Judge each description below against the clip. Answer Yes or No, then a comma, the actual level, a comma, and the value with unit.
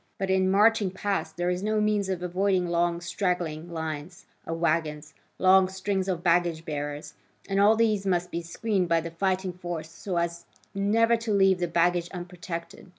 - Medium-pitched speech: Yes, medium, 180 Hz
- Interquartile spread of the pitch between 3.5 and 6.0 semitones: No, narrow, 2.5 semitones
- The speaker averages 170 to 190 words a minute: Yes, average, 175 wpm